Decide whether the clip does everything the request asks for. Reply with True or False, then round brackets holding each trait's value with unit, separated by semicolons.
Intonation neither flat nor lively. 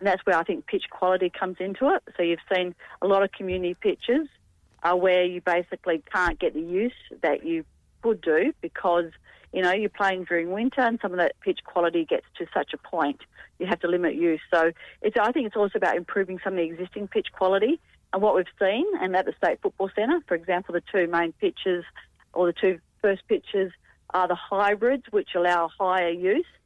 True (3.8 semitones)